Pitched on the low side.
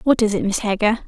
No: high, 215 Hz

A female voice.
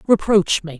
No: male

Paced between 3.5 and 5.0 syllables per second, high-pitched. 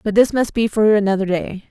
No: 5.8 syllables/s; high, 205 Hz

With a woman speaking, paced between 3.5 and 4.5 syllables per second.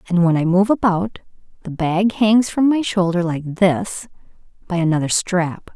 Yes: female; 4.4 syllables/s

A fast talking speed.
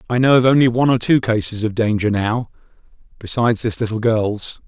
No: average, 190 wpm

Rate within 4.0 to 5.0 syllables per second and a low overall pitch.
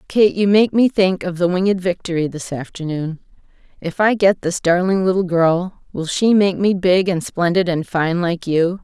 No: 4.7 syllables/s; medium, 180 Hz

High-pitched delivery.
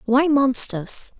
Yes: very high, 255 Hz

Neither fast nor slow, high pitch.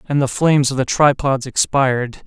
No: average, 185 wpm; low, 135 Hz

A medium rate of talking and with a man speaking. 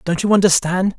Yes: average, 185 wpm; male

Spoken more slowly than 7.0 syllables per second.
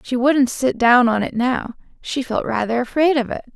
Yes: 4.8 syllables/s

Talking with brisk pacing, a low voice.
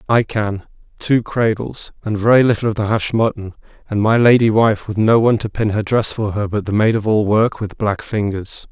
Yes: fast, 220 wpm; low, 110 Hz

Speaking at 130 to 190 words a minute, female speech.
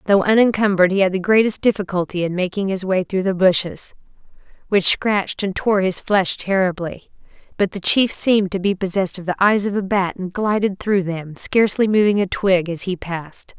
No: average, 200 wpm; female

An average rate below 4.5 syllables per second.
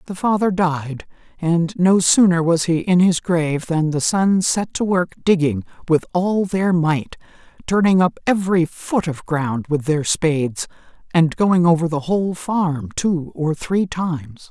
Yes: 4.1 syllables/s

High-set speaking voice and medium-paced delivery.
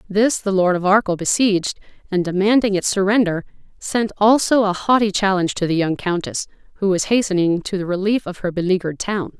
Yes: high, 195 Hz; average, 185 wpm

